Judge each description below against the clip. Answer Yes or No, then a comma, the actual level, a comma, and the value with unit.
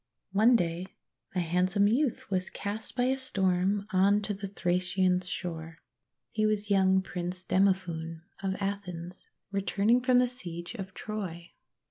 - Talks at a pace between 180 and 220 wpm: No, average, 140 wpm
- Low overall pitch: No, high, 190 Hz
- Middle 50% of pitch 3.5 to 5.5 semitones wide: No, narrow, 2.5 semitones